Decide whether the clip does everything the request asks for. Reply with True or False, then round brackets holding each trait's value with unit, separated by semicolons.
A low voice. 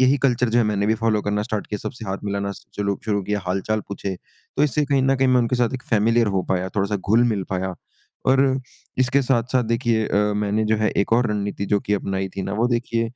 True (110 Hz)